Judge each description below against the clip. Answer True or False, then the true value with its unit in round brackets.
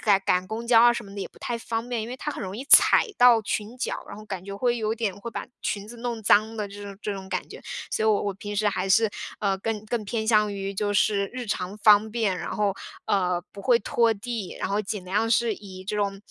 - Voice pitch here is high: True (210 Hz)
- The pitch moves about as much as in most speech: False (2.3 semitones)